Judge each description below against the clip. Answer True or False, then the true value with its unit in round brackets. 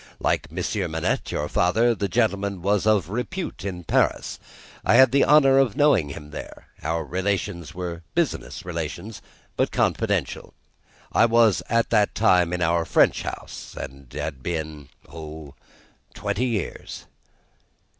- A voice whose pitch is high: False (90 Hz)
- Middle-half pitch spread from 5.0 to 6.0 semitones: True (5.5 semitones)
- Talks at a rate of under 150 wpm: True (140 wpm)